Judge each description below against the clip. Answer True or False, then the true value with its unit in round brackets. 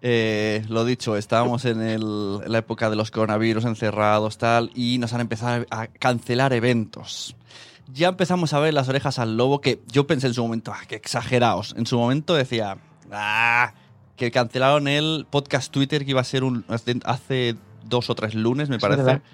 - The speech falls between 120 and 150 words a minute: False (185 wpm)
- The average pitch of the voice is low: True (120 Hz)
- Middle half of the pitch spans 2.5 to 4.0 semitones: True (2.8 semitones)